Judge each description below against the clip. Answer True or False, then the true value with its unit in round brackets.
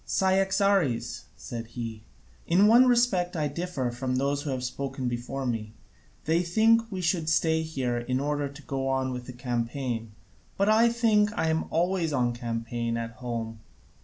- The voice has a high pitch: False (140 Hz)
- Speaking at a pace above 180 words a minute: False (165 wpm)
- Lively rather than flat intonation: True (6.8 semitones)